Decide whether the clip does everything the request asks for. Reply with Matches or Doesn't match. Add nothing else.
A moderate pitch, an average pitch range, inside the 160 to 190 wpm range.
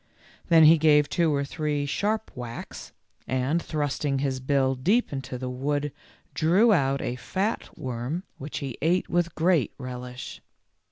Doesn't match